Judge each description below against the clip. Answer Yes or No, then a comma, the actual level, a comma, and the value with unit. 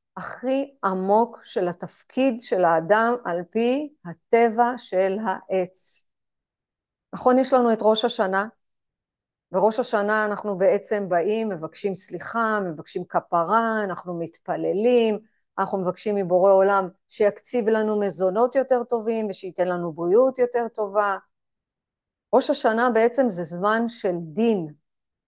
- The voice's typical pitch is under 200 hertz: No, high, 210 Hz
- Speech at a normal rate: Yes, average, 115 wpm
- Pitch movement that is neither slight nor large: Yes, average, 3.8 semitones